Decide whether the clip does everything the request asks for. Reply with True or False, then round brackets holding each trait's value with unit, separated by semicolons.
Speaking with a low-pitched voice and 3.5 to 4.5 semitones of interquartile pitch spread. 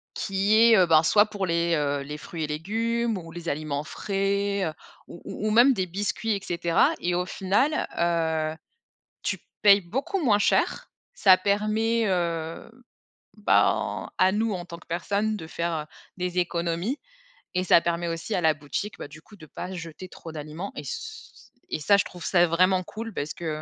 False (180 Hz; 3.8 semitones)